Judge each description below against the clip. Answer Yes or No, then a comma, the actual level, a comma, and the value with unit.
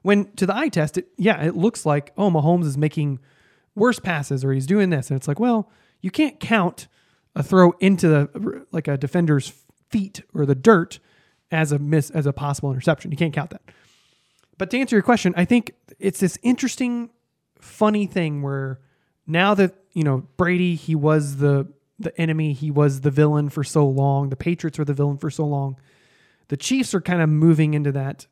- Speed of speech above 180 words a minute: Yes, average, 200 wpm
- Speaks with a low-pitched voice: No, medium, 160 Hz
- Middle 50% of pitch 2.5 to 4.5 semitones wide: No, average, 4.9 semitones